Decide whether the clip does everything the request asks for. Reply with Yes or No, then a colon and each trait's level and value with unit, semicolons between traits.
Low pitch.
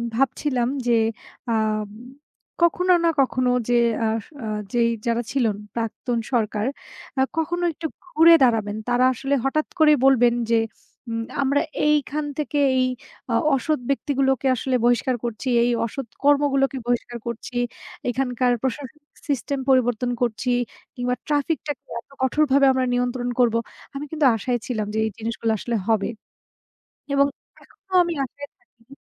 No: very high, 255 Hz